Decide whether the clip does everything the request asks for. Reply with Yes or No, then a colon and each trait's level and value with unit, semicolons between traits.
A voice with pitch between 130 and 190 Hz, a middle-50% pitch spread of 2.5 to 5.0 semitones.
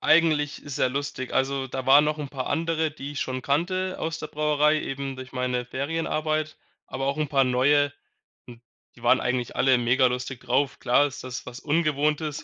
Yes: medium, 140 Hz; average, 2.9 semitones